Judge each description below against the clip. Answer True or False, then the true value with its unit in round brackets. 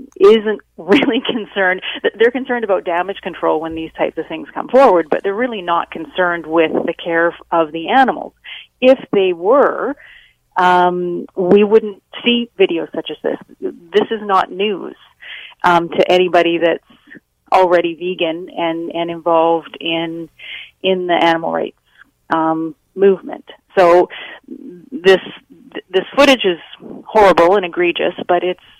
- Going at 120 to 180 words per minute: True (140 wpm)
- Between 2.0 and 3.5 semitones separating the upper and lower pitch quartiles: False (4.8 semitones)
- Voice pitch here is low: False (180 Hz)